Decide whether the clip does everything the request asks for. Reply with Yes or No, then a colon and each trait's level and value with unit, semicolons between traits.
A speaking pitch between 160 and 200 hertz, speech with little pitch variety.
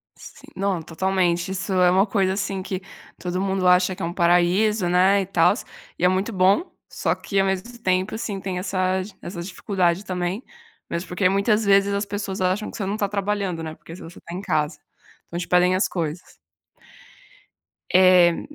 Yes: medium, 185 Hz; narrow, 1.8 semitones